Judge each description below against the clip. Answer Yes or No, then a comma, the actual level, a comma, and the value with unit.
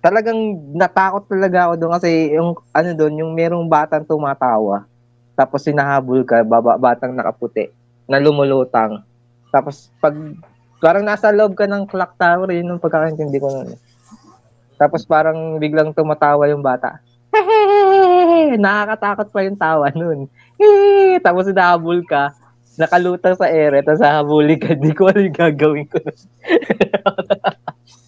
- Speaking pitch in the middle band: Yes, medium, 155 Hz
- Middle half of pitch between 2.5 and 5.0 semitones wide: No, wide, 5.5 semitones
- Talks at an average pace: Yes, average, 135 wpm